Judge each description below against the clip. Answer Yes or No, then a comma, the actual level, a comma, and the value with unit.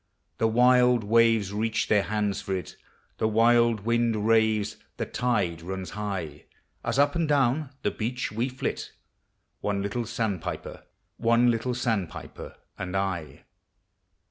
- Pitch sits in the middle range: No, low, 110 Hz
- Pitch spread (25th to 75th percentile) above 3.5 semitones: No, average, 3.1 semitones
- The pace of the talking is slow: Yes, slow, 125 wpm